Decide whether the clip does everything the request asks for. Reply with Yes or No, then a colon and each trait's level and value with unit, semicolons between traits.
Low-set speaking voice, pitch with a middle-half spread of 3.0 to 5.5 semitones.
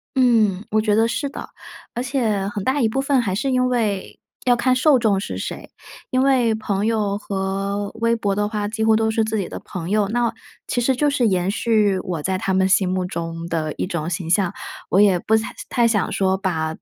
No: high, 210 Hz; average, 3.6 semitones